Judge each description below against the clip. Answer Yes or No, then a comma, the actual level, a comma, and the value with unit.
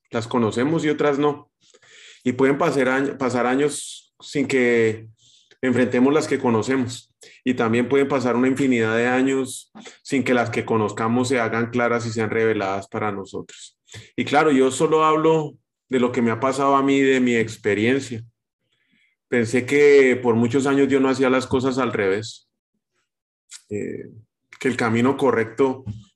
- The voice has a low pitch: Yes, low, 125 Hz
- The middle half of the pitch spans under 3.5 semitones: Yes, average, 2.8 semitones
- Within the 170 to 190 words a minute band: No, average, 160 wpm